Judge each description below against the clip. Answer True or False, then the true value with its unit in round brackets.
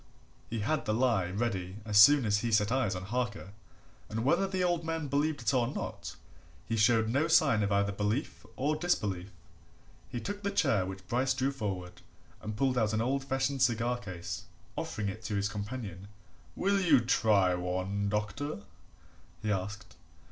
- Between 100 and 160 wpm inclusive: False (175 wpm)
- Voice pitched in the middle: False (110 Hz)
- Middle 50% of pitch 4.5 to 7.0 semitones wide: True (5.0 semitones)